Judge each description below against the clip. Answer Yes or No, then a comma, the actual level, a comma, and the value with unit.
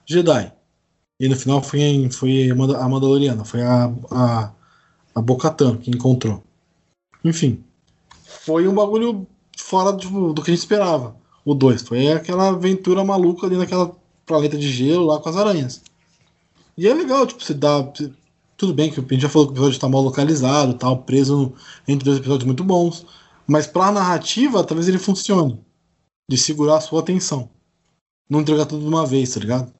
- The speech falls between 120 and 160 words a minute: No, average, 180 wpm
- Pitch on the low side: No, medium, 150 Hz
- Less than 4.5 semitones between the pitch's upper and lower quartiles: No, average, 5.0 semitones